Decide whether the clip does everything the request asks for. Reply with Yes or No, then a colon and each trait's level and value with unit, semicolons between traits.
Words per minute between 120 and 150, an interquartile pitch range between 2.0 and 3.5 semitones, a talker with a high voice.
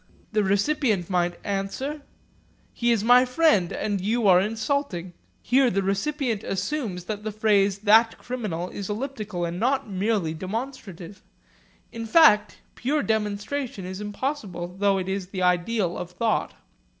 No: average, 140 wpm; average, 4.1 semitones; high, 210 Hz